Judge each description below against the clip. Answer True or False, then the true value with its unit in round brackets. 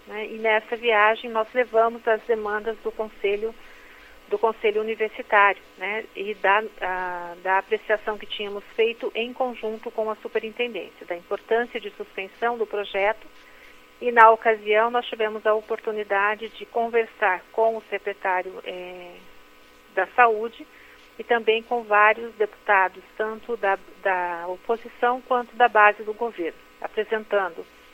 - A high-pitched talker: True (215 Hz)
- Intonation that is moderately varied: False (2.2 semitones)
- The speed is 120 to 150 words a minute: True (135 wpm)